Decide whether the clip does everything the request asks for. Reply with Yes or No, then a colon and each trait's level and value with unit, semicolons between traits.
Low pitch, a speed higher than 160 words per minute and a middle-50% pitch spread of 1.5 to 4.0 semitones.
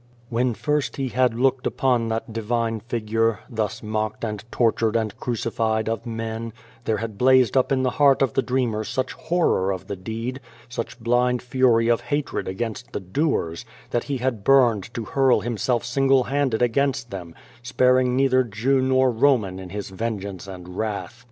Yes: low, 115 Hz; average, 170 wpm; average, 2.9 semitones